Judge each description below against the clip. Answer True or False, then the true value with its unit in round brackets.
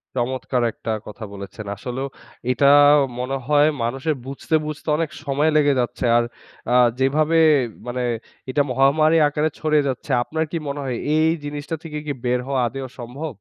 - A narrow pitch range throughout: False (3.3 semitones)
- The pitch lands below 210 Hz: True (140 Hz)